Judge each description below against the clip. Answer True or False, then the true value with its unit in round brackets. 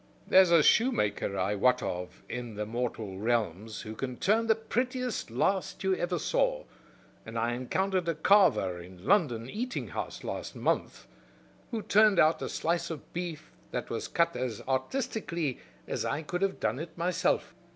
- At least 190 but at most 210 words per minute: False (170 wpm)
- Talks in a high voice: False (155 Hz)